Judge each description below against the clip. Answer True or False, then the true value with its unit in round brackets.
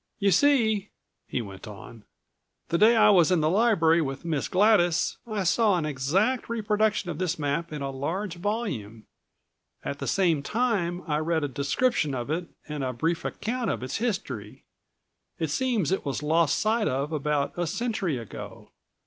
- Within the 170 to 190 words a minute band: True (175 wpm)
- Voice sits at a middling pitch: True (170 Hz)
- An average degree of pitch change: False (6.6 semitones)